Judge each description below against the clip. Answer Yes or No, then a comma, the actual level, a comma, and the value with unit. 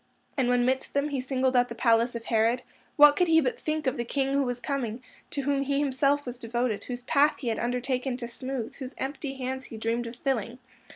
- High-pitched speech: Yes, very high, 255 Hz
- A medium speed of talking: No, fast, 230 wpm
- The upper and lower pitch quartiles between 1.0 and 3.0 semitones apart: Yes, narrow, 2.5 semitones